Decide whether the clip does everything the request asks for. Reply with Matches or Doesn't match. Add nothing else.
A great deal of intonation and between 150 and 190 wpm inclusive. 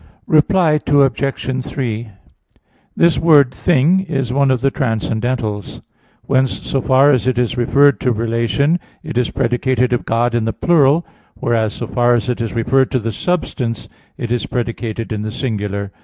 Doesn't match